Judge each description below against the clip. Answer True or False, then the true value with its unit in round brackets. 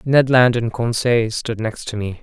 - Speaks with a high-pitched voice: False (115 Hz)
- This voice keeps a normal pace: False (215 wpm)